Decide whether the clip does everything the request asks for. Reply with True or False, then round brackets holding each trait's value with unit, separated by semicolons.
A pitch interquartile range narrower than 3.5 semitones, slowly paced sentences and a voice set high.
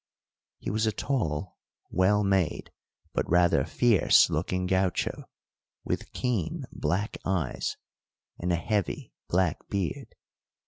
False (2.9 semitones; 110 wpm; 95 Hz)